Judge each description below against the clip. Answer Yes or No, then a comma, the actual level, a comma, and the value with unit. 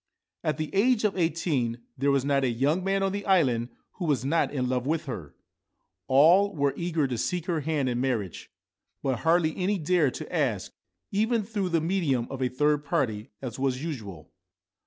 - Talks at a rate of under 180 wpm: No, average, 190 wpm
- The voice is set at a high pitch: No, medium, 150 Hz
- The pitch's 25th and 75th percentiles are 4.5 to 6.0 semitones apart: Yes, wide, 5.6 semitones